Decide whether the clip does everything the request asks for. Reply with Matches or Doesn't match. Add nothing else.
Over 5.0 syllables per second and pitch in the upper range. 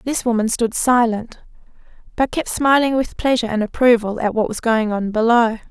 Matches